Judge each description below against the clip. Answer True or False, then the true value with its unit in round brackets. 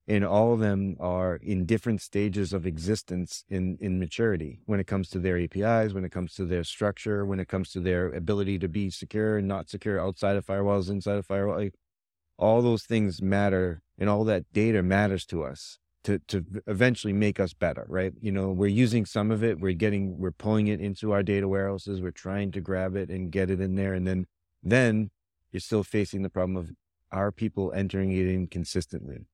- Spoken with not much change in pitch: True (2.1 semitones)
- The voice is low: True (95 Hz)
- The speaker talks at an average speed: False (210 wpm)